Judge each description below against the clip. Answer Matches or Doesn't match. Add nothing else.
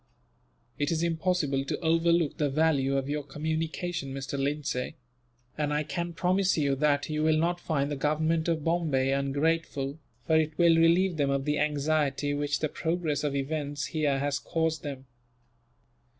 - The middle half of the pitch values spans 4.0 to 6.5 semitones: Doesn't match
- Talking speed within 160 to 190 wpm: Matches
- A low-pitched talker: Doesn't match